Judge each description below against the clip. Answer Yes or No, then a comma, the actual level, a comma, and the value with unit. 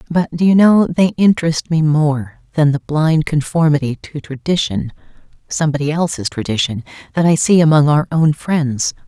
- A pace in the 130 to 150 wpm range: Yes, average, 145 wpm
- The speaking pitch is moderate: Yes, medium, 150 Hz